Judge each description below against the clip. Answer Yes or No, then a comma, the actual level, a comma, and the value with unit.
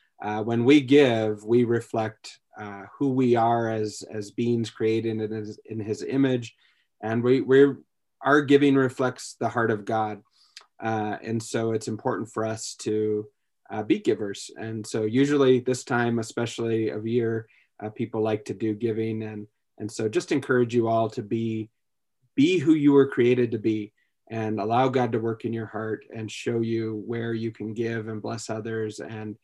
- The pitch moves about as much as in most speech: No, narrow, 2.0 semitones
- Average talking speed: Yes, average, 180 wpm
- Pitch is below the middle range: Yes, low, 115 Hz